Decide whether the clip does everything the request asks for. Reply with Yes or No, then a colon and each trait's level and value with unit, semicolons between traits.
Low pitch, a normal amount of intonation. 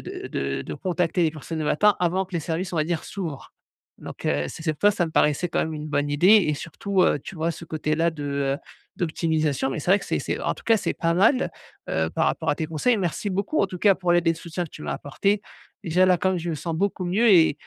No: medium, 165 Hz; average, 3.4 semitones